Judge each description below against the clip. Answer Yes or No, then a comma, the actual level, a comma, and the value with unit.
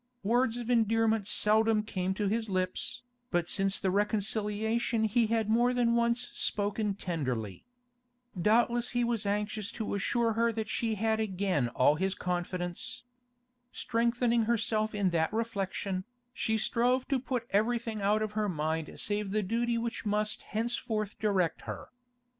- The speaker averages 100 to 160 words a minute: Yes, average, 145 wpm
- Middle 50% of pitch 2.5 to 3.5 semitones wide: Yes, average, 2.9 semitones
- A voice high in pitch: Yes, high, 215 Hz